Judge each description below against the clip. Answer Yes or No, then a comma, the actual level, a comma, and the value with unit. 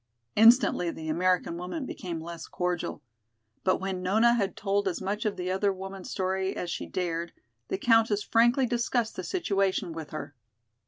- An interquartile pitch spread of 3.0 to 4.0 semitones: Yes, average, 3.5 semitones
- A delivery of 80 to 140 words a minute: No, average, 165 wpm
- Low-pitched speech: No, high, 190 Hz